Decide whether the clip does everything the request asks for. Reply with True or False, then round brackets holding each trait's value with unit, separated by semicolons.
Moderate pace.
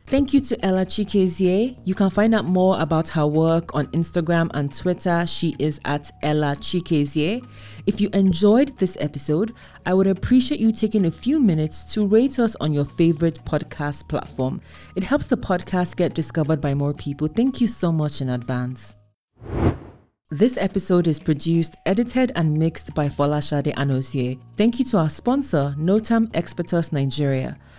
True (165 wpm)